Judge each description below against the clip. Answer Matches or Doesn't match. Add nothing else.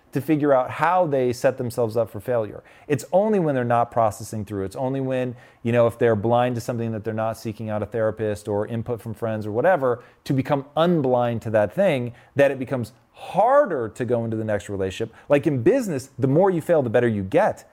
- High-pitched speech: Doesn't match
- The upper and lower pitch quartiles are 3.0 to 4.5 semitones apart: Matches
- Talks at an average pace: Doesn't match